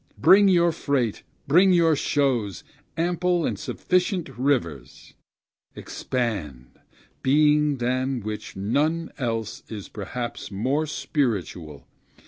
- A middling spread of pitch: No, wide, 6.7 semitones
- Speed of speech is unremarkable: No, slow, 100 wpm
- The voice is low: Yes, low, 130 Hz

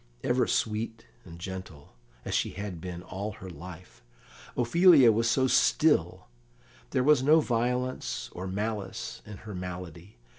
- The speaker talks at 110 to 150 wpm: Yes, average, 140 wpm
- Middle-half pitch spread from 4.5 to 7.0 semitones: Yes, average, 5.1 semitones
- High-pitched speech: No, low, 105 Hz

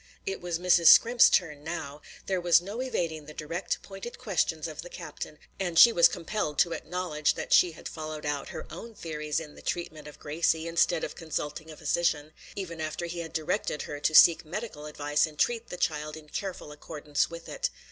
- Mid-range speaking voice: Yes, medium, 165 Hz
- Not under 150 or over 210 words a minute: Yes, average, 200 wpm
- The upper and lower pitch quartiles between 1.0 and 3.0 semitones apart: Yes, average, 2.7 semitones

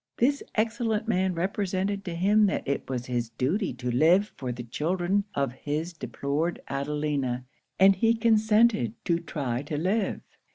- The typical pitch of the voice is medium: Yes, medium, 175 Hz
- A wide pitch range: Yes, wide, 6.8 semitones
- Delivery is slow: No, average, 155 wpm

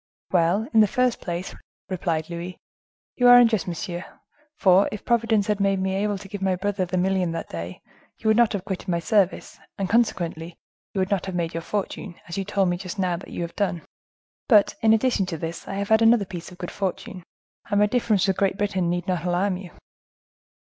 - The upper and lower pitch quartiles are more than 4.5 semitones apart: No, average, 2.7 semitones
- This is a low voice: No, high, 190 Hz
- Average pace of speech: No, fast, 215 wpm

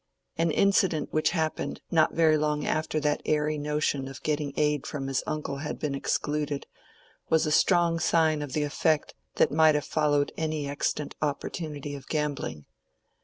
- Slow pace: No, average, 165 wpm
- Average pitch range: No, narrow, 1.4 semitones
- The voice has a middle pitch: Yes, medium, 150 Hz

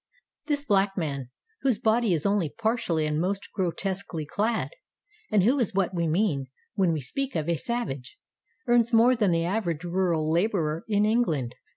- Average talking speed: Yes, average, 170 wpm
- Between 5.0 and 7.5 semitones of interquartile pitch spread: Yes, wide, 5.6 semitones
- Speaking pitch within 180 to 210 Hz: Yes, high, 190 Hz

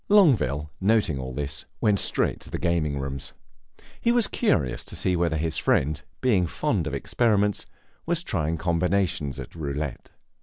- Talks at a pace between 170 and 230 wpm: No, average, 155 wpm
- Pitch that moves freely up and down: Yes, wide, 6.0 semitones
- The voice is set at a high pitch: No, very low, 85 Hz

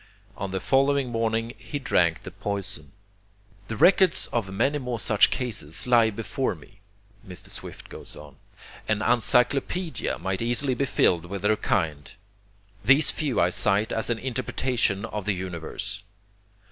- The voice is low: Yes, low, 110 Hz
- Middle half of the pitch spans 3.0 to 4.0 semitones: No, average, 4.7 semitones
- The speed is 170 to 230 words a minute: No, average, 145 wpm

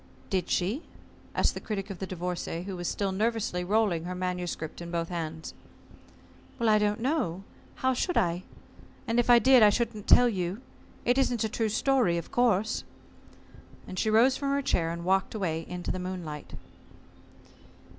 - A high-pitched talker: Yes, high, 195 Hz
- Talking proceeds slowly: No, average, 170 wpm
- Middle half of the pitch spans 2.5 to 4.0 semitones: No, average, 4.7 semitones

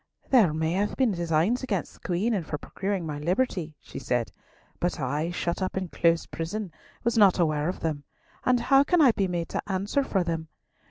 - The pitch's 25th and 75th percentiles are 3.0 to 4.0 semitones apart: No, average, 4.7 semitones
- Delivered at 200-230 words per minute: Yes, fast, 205 wpm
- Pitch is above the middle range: No, medium, 180 Hz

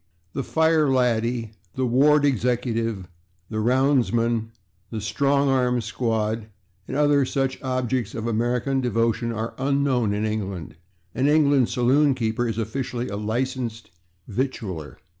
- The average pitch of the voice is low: Yes, low, 120 Hz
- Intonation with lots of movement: No, average, 3.1 semitones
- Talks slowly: Yes, slow, 125 wpm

